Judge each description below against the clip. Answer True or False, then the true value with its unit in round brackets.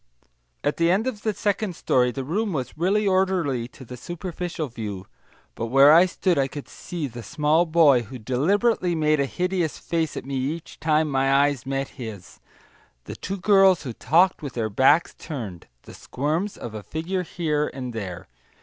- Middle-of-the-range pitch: True (150 Hz)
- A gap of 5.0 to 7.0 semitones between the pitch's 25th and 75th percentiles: True (5.6 semitones)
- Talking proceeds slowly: False (185 wpm)